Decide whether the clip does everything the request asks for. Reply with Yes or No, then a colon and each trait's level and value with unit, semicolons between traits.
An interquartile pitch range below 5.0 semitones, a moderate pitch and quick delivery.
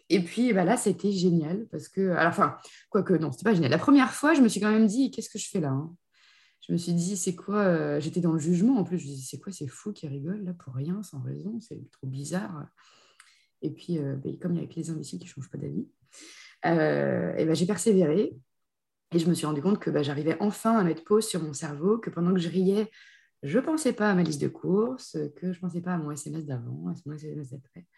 No: average, 5.3 semitones; medium, 175 Hz; fast, 265 wpm